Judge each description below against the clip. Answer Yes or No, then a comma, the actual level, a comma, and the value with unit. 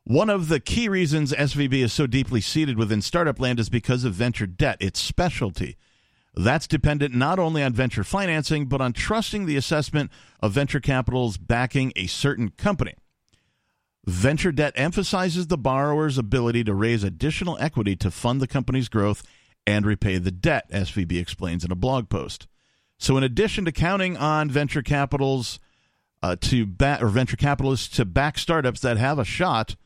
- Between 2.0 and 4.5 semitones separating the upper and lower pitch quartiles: No, average, 5.0 semitones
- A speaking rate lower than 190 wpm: Yes, average, 170 wpm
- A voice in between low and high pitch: No, low, 130 Hz